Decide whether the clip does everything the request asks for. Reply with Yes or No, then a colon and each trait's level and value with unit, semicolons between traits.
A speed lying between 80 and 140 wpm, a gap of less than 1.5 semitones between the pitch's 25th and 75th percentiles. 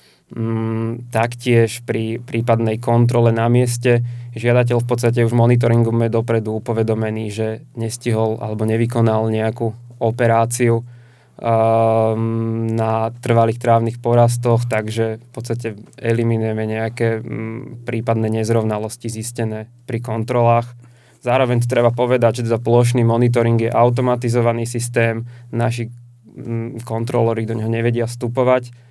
Yes: slow, 110 wpm; narrow, 1.1 semitones